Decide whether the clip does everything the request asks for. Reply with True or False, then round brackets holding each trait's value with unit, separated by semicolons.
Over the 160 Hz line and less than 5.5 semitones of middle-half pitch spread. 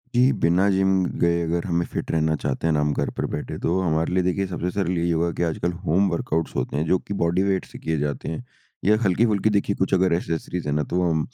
False (85 Hz; 2.7 semitones)